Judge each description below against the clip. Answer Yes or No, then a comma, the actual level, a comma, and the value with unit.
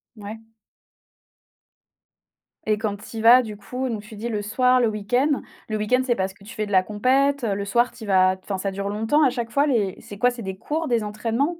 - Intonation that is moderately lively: Yes, average, 3.6 semitones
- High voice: Yes, high, 220 Hz